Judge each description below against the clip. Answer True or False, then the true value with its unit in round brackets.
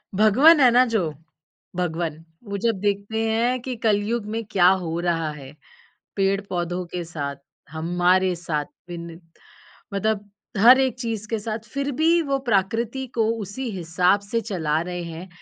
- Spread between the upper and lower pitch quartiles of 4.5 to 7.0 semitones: True (4.8 semitones)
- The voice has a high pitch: True (195 Hz)